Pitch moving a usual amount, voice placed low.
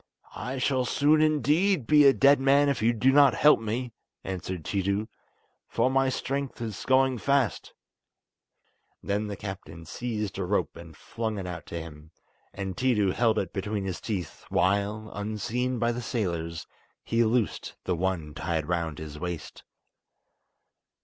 No: wide, 5.7 semitones; low, 110 Hz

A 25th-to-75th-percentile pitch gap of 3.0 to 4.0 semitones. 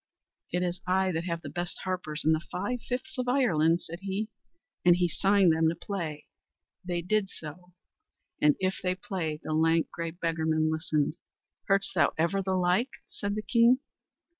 Yes: average, 3.3 semitones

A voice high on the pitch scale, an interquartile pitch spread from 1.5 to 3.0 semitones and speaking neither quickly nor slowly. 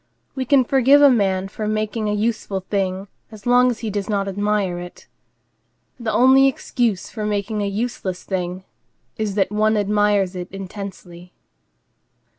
Yes: high, 210 Hz; narrow, 2.6 semitones; average, 155 wpm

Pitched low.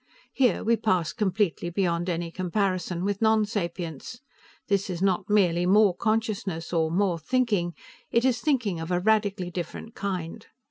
No: high, 190 Hz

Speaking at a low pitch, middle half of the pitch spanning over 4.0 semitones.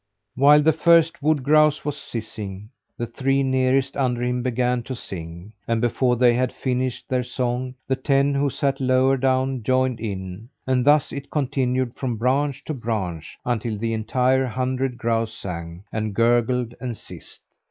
No: low, 125 Hz; average, 2.7 semitones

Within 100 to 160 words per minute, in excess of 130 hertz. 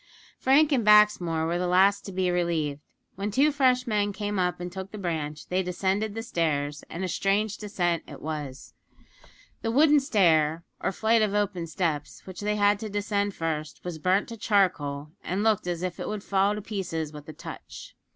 No: average, 195 wpm; high, 190 Hz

